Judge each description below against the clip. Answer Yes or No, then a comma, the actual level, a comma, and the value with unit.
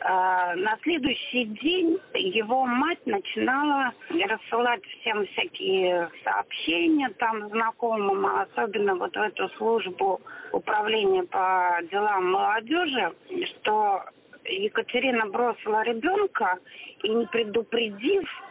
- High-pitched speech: Yes, very high, 255 Hz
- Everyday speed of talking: No, slow, 90 wpm